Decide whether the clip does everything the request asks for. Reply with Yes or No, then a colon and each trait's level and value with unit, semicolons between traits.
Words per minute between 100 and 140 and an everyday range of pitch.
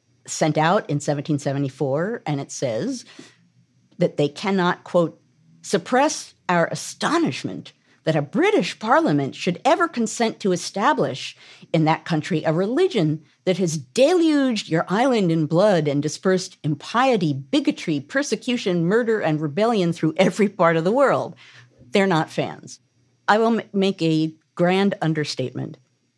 No: slow, 135 wpm; wide, 5.7 semitones